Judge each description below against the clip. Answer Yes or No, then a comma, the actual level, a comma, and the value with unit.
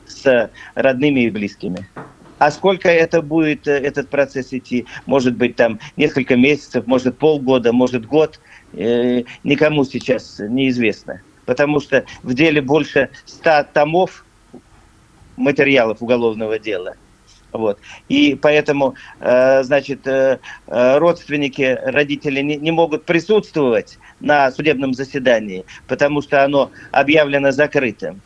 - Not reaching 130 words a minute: Yes, slow, 110 wpm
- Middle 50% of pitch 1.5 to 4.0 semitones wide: Yes, average, 2.9 semitones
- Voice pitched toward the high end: No, medium, 140 Hz